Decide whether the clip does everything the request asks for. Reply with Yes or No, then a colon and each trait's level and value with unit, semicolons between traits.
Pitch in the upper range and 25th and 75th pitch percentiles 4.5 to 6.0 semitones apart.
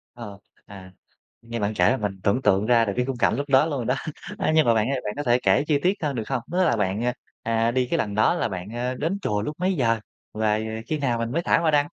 No: low, 120 Hz; average, 4.9 semitones